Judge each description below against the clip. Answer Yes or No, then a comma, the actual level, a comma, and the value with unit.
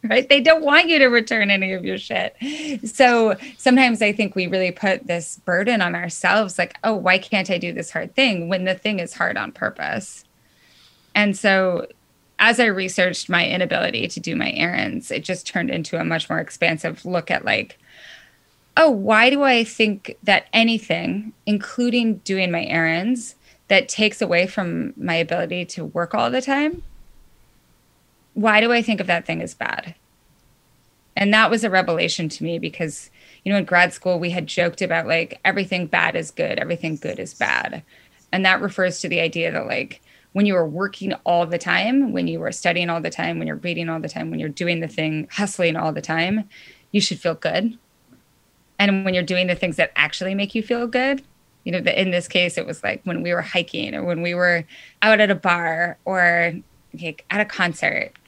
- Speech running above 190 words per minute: Yes, average, 200 wpm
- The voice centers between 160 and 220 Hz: Yes, high, 190 Hz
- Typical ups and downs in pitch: Yes, average, 4.3 semitones